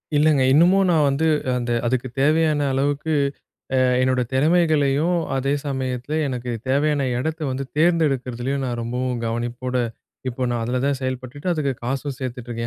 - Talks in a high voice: No, low, 135 Hz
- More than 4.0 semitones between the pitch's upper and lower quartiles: No, average, 3.2 semitones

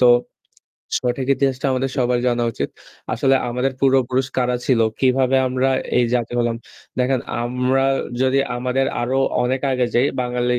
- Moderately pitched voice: No, low, 125 Hz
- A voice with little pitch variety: Yes, narrow, 1.3 semitones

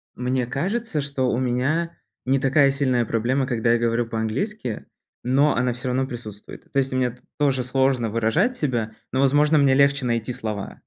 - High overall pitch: No, low, 130 Hz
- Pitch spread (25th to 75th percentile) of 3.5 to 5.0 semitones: No, average, 2.9 semitones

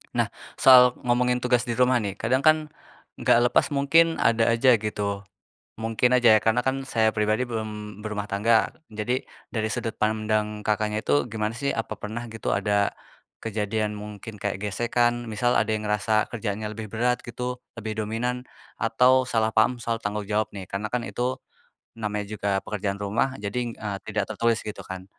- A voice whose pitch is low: Yes, low, 110 Hz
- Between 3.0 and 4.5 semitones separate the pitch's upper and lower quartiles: No, narrow, 2.4 semitones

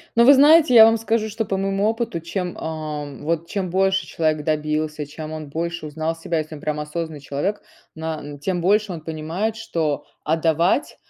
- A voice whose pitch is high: No, medium, 165 Hz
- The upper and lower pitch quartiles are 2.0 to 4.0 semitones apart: No, average, 4.4 semitones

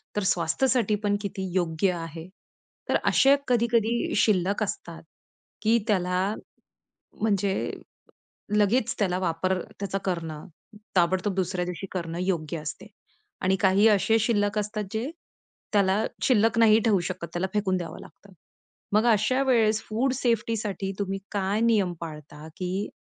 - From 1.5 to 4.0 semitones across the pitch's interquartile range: Yes, average, 3.3 semitones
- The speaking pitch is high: Yes, high, 200 Hz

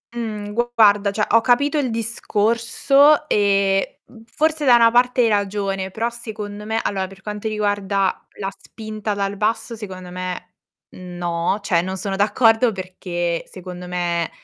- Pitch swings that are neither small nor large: Yes, average, 3.2 semitones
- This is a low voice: No, high, 205 Hz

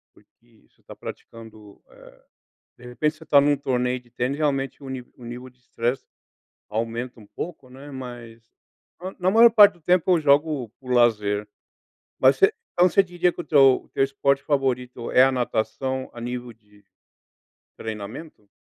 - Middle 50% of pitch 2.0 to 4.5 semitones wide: Yes, average, 3.7 semitones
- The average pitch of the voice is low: Yes, low, 130 Hz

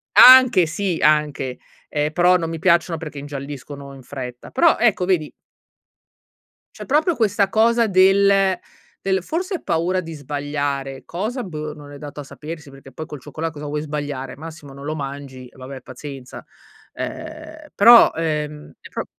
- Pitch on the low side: No, medium, 155 Hz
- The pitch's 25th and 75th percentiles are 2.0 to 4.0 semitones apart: No, average, 5.2 semitones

